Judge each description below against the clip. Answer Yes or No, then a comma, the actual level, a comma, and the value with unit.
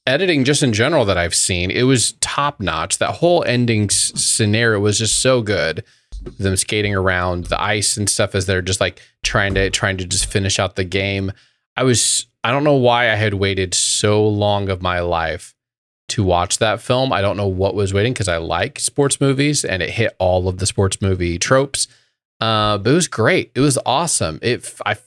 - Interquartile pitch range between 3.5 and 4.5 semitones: Yes, average, 4.1 semitones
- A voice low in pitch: Yes, low, 105 Hz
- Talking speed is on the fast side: Yes, fast, 210 wpm